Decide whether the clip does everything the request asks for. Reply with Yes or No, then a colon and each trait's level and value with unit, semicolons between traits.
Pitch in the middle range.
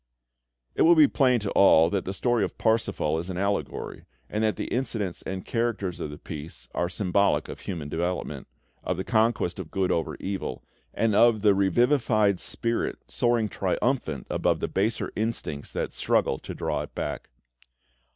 No: low, 100 Hz